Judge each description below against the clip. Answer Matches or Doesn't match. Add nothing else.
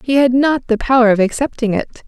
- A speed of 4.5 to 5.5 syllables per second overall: Doesn't match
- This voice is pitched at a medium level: Doesn't match